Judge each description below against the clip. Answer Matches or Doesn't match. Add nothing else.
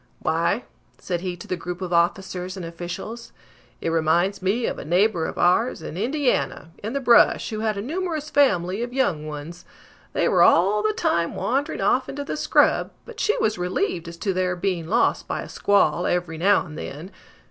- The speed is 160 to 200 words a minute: Matches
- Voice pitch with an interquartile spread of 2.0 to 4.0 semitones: Doesn't match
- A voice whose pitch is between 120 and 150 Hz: Doesn't match